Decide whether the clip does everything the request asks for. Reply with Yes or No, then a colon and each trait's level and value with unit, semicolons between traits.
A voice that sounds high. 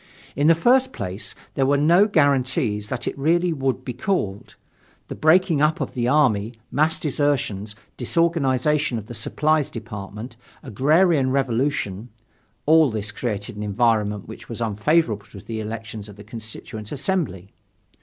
No: low, 125 Hz